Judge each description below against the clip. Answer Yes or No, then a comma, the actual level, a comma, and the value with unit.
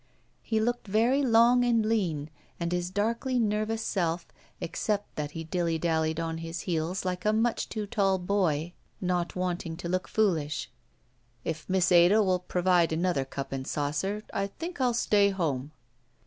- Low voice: No, medium, 180 Hz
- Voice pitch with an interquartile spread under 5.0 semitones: Yes, average, 4.5 semitones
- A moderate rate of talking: Yes, average, 160 wpm